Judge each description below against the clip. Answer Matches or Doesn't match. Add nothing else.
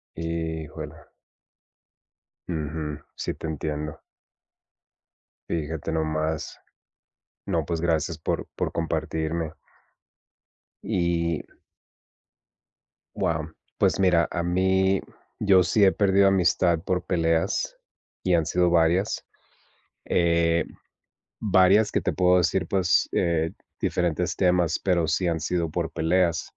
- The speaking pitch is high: Doesn't match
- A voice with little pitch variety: Matches